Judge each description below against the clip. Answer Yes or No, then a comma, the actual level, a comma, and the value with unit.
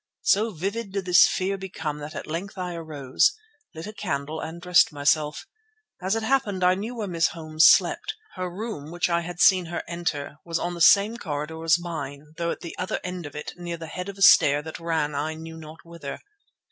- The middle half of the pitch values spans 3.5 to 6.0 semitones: No, average, 3.1 semitones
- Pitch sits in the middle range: Yes, medium, 170 Hz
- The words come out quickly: Yes, fast, 215 wpm